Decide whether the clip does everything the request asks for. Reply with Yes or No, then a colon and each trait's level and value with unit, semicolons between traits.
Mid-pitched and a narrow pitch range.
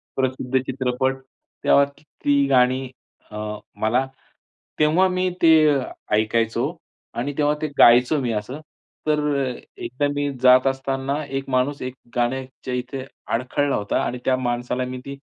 No: low, 130 Hz; narrow, 2.1 semitones